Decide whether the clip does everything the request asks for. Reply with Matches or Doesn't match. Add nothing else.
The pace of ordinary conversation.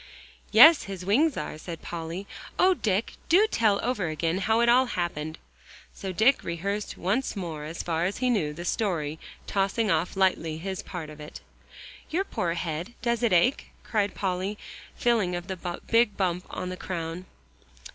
Matches